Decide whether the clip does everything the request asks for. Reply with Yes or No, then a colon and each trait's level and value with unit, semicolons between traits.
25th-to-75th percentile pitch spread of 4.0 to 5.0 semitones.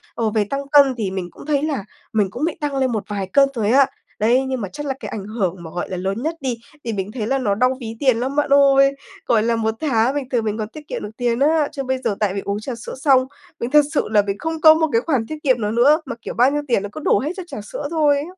Yes: average, 4.7 semitones